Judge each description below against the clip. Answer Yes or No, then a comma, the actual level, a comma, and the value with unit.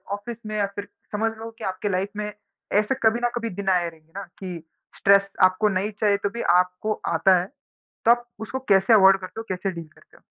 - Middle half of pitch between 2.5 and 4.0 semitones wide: Yes, average, 2.9 semitones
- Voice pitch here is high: Yes, high, 200 Hz